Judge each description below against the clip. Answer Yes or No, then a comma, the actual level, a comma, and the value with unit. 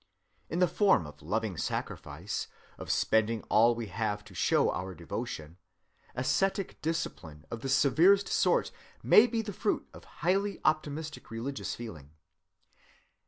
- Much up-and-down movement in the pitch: Yes, wide, 8.9 semitones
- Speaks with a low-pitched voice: Yes, low, 120 Hz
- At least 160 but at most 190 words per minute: No, slow, 135 wpm